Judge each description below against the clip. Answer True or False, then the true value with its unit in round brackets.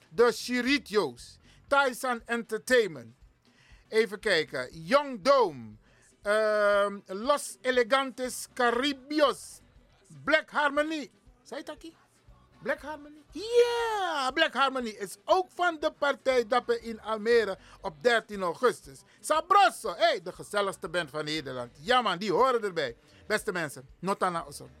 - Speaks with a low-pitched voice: False (240 Hz)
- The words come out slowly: True (125 wpm)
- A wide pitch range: True (6.3 semitones)